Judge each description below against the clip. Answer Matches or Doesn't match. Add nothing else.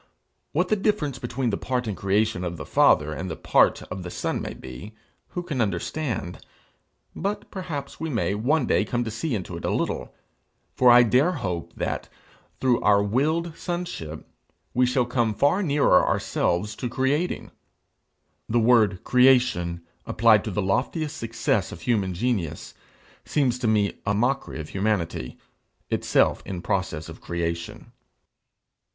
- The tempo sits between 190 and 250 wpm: Doesn't match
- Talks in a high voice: Doesn't match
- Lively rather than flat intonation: Matches